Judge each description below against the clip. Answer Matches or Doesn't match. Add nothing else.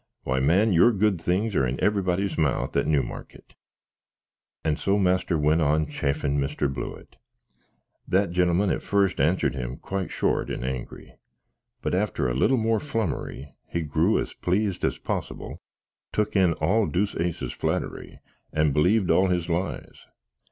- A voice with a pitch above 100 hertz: Doesn't match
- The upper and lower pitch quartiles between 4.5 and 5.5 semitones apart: Matches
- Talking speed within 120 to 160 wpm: Matches